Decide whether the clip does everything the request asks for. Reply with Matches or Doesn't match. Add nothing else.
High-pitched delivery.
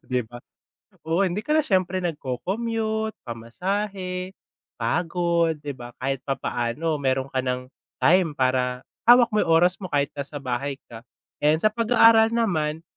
Doesn't match